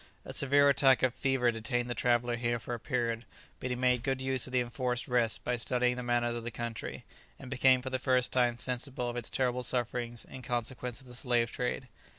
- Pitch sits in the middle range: No, low, 125 Hz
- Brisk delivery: Yes, fast, 220 wpm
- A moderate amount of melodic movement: No, narrow, 1.3 semitones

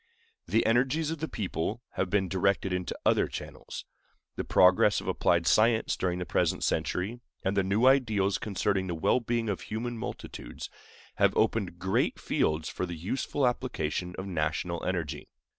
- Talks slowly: No, average, 160 wpm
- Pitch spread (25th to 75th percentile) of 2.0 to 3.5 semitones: No, average, 4.4 semitones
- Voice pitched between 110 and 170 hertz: No, very low, 95 Hz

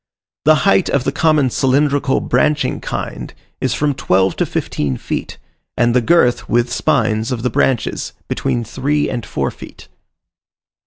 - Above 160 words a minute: No, average, 150 wpm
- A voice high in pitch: No, low, 130 Hz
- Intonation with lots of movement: No, average, 3.9 semitones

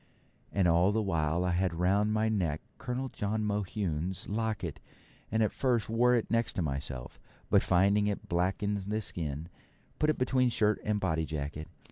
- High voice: No, low, 100 Hz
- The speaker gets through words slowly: No, average, 165 wpm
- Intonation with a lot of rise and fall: No, average, 4.3 semitones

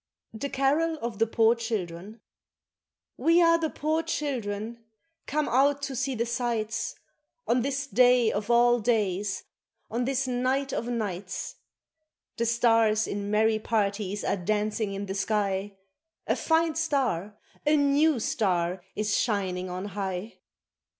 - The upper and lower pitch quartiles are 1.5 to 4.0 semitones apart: No, average, 4.8 semitones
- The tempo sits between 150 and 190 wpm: No, slow, 135 wpm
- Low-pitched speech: No, high, 230 Hz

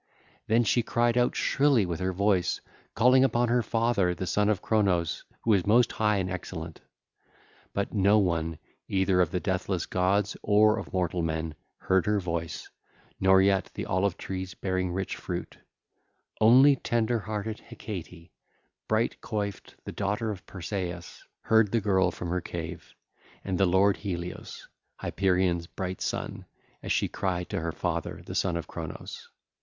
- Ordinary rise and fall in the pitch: Yes, average, 3.2 semitones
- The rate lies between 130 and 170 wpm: Yes, average, 160 wpm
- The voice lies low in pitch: Yes, very low, 95 Hz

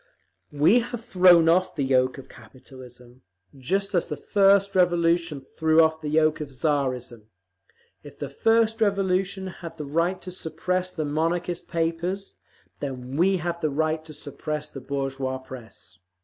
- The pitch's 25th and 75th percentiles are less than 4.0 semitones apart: No, average, 5.1 semitones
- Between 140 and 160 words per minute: Yes, average, 150 wpm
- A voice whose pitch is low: No, medium, 160 Hz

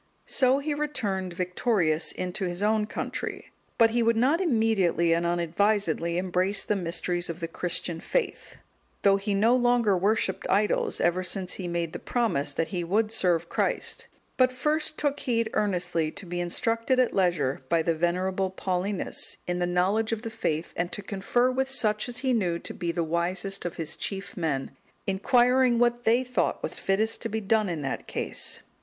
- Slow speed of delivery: No, average, 180 wpm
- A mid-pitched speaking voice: No, high, 195 Hz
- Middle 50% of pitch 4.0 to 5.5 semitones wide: Yes, average, 4.8 semitones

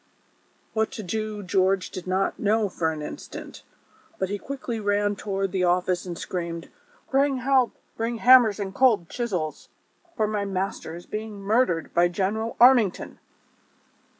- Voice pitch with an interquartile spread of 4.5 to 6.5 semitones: No, average, 3.5 semitones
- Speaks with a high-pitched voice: Yes, high, 205 Hz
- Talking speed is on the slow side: No, average, 155 wpm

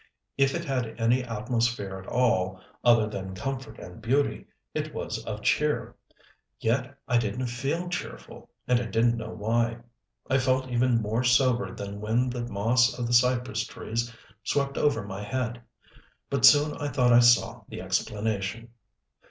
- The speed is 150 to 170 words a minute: Yes, average, 160 wpm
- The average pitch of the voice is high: No, low, 120 Hz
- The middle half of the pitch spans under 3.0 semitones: Yes, narrow, 2.5 semitones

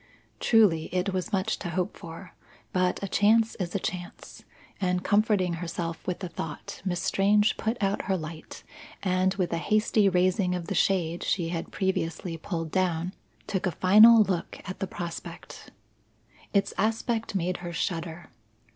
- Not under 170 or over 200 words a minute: No, average, 160 wpm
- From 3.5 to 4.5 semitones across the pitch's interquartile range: No, narrow, 2.6 semitones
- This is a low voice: No, medium, 185 Hz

